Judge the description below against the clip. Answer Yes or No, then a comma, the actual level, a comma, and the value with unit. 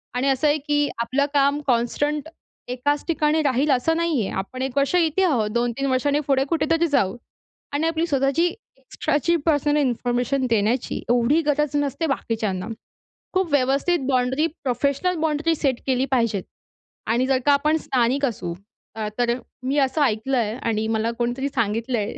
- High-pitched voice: Yes, very high, 270 Hz